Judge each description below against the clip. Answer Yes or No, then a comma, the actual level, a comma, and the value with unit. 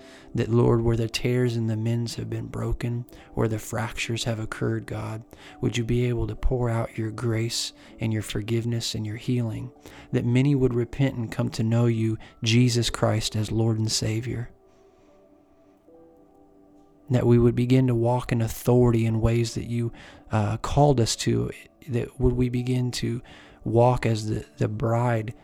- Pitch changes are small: Yes, narrow, 1.8 semitones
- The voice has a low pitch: Yes, low, 115 Hz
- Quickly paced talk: No, average, 170 wpm